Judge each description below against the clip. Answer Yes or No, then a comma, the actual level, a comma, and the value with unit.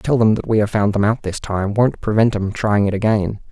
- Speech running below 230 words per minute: No, fast, 290 wpm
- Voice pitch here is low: Yes, low, 105 Hz